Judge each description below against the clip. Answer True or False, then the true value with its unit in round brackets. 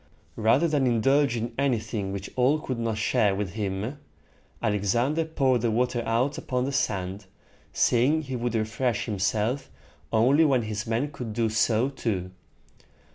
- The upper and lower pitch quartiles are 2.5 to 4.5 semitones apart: True (3.7 semitones)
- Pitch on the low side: True (115 Hz)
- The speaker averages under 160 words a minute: True (150 wpm)